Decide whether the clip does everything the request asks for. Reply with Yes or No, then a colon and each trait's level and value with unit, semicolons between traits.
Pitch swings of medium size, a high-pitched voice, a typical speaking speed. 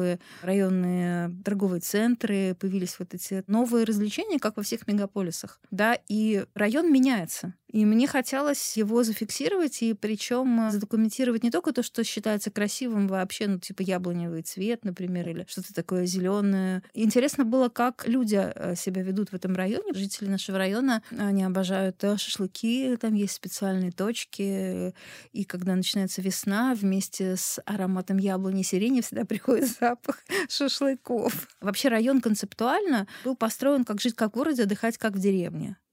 Yes: average, 4.0 semitones; high, 210 Hz; average, 145 wpm